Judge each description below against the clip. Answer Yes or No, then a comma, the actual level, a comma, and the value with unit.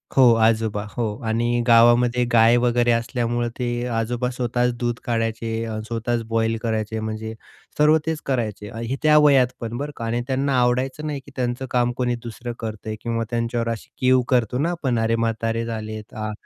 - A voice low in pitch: Yes, low, 120 Hz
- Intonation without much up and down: Yes, narrow, 1.6 semitones